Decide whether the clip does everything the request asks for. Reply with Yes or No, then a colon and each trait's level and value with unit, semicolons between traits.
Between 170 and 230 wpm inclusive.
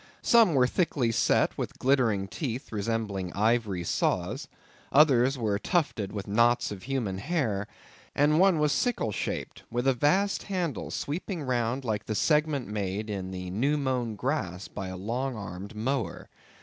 No: average, 155 wpm